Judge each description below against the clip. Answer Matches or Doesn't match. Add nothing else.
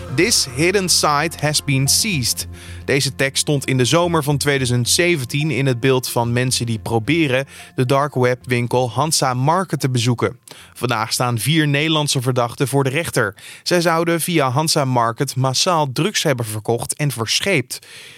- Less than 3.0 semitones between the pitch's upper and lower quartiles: Doesn't match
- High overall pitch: Doesn't match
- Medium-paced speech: Matches